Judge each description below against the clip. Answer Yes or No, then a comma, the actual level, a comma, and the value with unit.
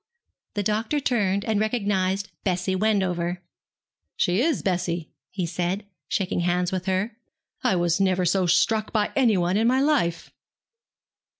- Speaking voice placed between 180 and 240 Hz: Yes, high, 190 Hz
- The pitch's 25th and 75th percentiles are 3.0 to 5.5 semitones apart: Yes, average, 3.3 semitones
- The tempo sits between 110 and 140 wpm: Yes, slow, 135 wpm